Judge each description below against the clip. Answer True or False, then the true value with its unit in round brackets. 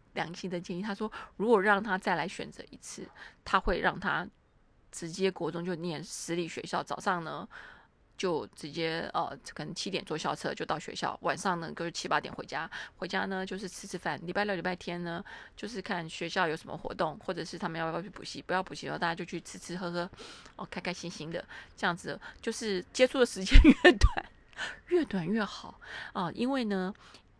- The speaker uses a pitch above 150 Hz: True (185 Hz)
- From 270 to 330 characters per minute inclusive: True (300 characters per minute)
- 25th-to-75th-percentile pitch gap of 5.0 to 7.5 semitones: False (2.9 semitones)